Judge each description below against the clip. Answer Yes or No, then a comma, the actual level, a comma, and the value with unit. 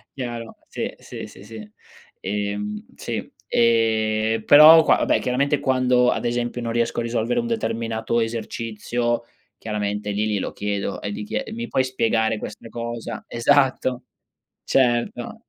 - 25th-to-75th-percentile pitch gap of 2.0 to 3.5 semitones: Yes, narrow, 2.4 semitones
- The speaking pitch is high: No, low, 115 Hz